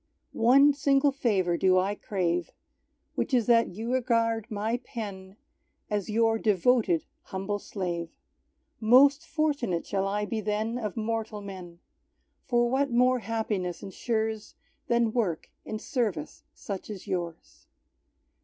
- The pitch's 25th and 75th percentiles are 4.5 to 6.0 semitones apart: No, average, 3.9 semitones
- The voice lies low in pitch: No, high, 220 Hz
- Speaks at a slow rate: Yes, slow, 125 wpm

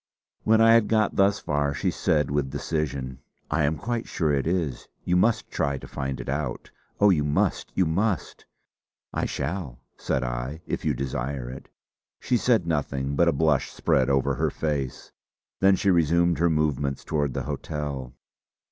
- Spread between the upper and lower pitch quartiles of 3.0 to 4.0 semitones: No, average, 4.5 semitones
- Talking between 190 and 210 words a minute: No, average, 175 wpm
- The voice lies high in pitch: No, very low, 75 Hz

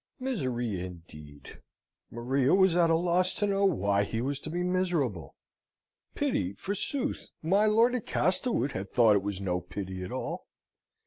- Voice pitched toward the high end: No, low, 135 Hz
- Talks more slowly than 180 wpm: Yes, average, 155 wpm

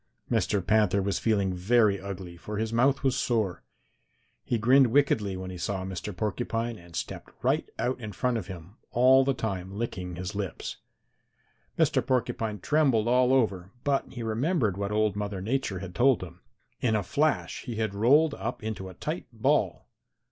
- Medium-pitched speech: No, low, 110 Hz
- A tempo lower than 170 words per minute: No, average, 175 wpm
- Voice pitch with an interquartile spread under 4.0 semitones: No, average, 4.4 semitones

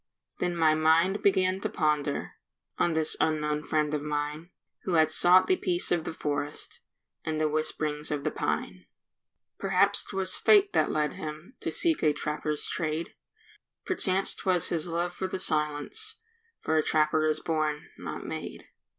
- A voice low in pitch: No, medium, 155 Hz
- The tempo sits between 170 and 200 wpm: No, average, 160 wpm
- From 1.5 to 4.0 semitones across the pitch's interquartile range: Yes, average, 2.9 semitones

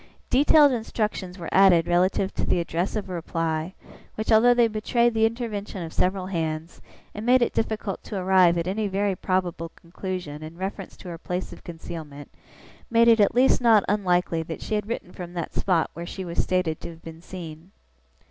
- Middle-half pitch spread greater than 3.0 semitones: Yes, average, 4.1 semitones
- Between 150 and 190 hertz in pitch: Yes, medium, 185 Hz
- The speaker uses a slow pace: No, average, 195 wpm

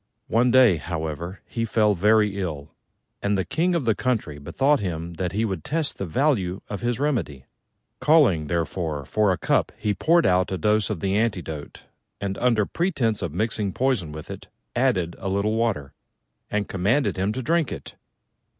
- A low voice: Yes, low, 100 Hz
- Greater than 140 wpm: Yes, average, 180 wpm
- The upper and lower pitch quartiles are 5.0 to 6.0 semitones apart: Yes, average, 5.3 semitones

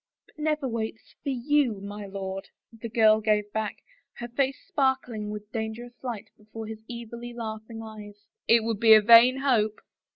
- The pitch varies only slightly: Yes, narrow, 2.2 semitones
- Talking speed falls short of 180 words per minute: No, average, 185 wpm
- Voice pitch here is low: No, high, 225 Hz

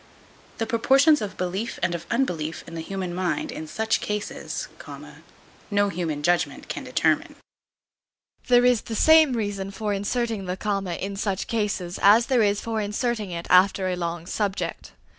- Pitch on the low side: No, high, 200 Hz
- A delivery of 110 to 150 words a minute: No, average, 160 wpm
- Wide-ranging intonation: No, average, 3.8 semitones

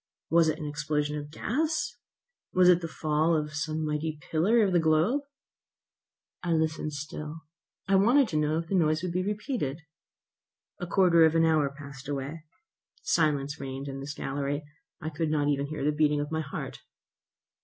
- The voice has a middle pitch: Yes, medium, 155 Hz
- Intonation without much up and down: Yes, narrow, 2.3 semitones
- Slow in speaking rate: No, average, 175 wpm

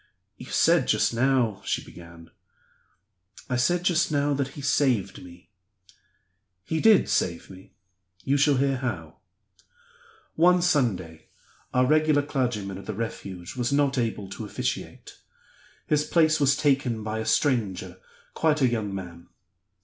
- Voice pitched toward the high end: No, low, 125 Hz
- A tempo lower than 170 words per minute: Yes, average, 140 wpm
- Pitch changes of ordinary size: No, wide, 6.8 semitones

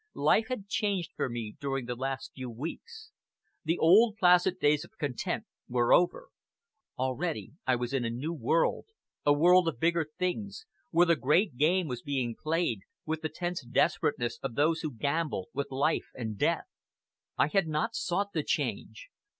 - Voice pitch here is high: No, medium, 155 Hz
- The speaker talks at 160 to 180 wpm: Yes, average, 170 wpm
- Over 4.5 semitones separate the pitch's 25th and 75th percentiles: Yes, wide, 5.5 semitones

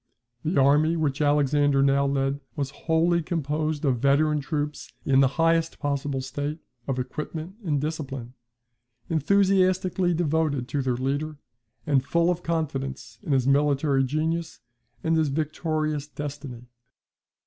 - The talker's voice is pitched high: No, medium, 150 Hz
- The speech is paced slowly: Yes, slow, 130 wpm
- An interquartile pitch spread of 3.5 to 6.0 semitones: No, average, 2.8 semitones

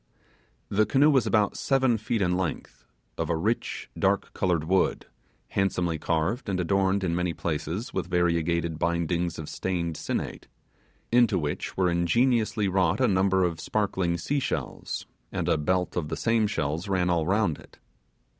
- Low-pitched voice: Yes, very low, 90 Hz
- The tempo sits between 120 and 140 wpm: No, average, 155 wpm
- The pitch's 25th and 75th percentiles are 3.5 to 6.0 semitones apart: Yes, average, 3.9 semitones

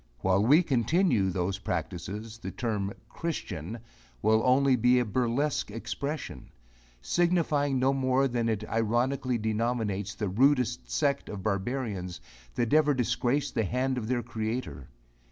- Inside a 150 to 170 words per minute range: No, slow, 135 wpm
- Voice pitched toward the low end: Yes, low, 120 Hz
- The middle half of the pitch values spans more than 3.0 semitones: Yes, average, 4.1 semitones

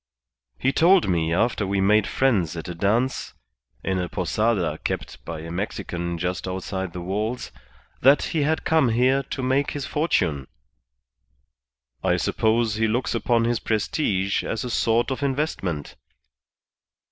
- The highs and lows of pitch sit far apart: Yes, wide, 6.2 semitones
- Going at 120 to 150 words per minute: Yes, average, 145 wpm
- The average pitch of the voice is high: No, low, 110 Hz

